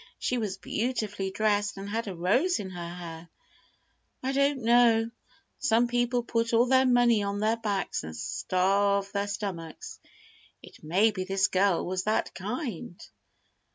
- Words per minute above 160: No, average, 155 wpm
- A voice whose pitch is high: Yes, high, 205 Hz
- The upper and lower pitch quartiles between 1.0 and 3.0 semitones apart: No, average, 3.9 semitones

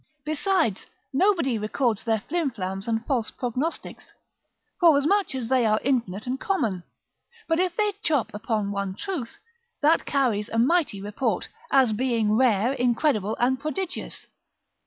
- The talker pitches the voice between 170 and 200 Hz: No, very high, 250 Hz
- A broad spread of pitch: Yes, wide, 6.2 semitones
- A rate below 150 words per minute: Yes, slow, 135 wpm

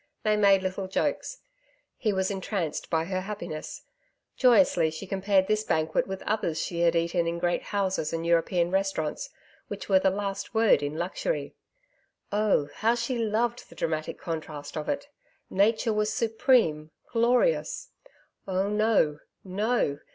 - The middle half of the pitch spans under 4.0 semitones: No, average, 4.3 semitones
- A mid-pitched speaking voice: No, high, 195 Hz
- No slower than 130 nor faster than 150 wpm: Yes, average, 145 wpm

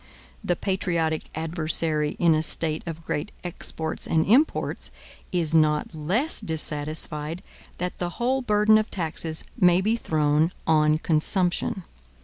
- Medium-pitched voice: Yes, medium, 165 Hz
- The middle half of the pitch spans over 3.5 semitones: No, average, 3.2 semitones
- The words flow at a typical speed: No, slow, 125 wpm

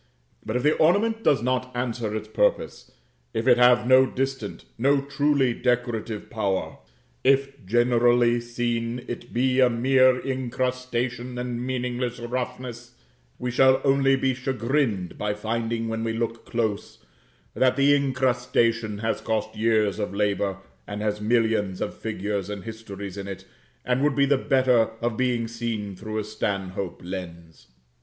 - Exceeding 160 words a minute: No, average, 150 wpm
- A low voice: Yes, low, 120 Hz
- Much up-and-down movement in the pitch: No, average, 2.9 semitones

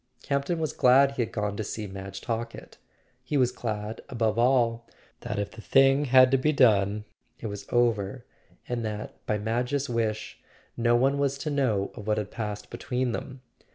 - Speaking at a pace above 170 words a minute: Yes, average, 185 wpm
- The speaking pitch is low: Yes, low, 115 Hz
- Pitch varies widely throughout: No, average, 3.8 semitones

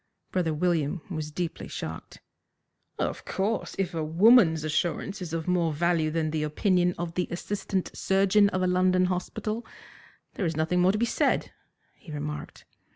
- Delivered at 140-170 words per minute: Yes, average, 160 wpm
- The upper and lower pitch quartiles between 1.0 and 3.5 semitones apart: Yes, average, 3.0 semitones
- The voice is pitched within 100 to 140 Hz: No, medium, 180 Hz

